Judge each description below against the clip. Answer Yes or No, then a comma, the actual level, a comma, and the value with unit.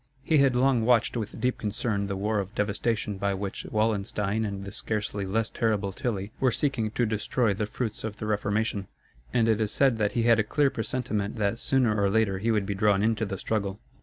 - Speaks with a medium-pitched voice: No, low, 110 Hz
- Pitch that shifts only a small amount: Yes, narrow, 2.3 semitones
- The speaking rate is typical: No, fast, 215 wpm